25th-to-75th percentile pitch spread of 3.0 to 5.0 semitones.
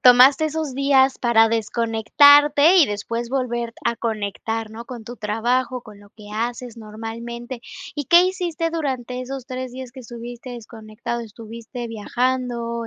No: narrow, 2.4 semitones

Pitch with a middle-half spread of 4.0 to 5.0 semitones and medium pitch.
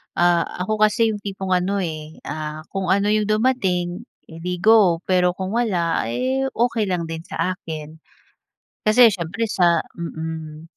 Yes: average, 4.3 semitones; medium, 180 Hz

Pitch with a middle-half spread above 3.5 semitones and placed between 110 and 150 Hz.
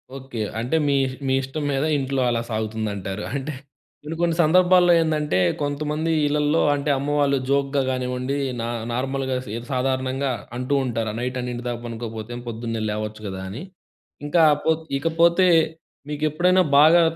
Yes: average, 4.2 semitones; low, 135 Hz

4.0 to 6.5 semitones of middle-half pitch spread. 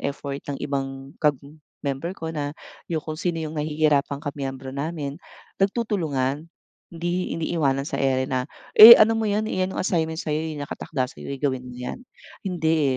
No: average, 3.4 semitones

